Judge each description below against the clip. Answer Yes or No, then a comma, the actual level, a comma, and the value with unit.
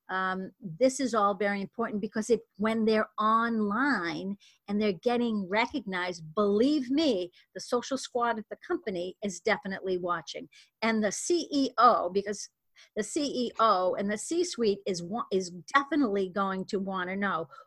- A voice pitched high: Yes, high, 210 Hz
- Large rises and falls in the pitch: No, average, 4.0 semitones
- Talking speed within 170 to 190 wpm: No, average, 150 wpm